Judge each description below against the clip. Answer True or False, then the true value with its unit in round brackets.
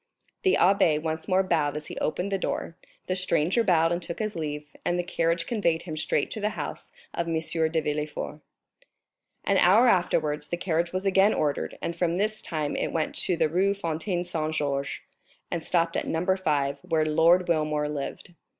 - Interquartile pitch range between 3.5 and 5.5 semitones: False (3.1 semitones)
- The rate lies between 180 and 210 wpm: True (185 wpm)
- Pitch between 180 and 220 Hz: False (170 Hz)